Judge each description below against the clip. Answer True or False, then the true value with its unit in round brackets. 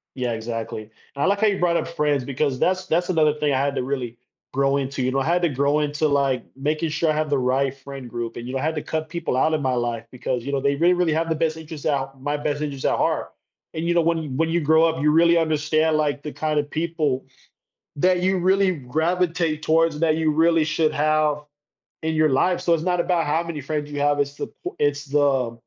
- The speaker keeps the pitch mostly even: False (3.0 semitones)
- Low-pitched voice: False (150 Hz)